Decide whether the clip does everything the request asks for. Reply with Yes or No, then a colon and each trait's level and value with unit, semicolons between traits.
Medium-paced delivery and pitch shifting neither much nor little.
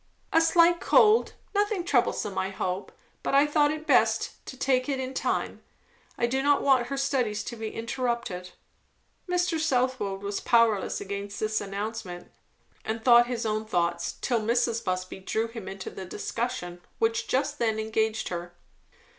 Yes: average, 155 wpm; average, 4.8 semitones